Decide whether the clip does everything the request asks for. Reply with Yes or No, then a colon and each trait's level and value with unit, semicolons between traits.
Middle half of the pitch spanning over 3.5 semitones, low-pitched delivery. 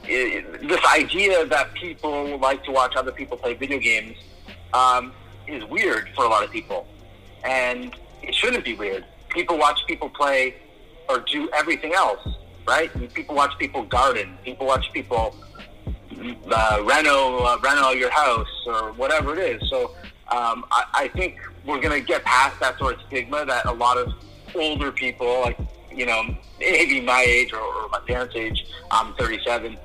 Yes: average, 4.6 semitones; low, 125 Hz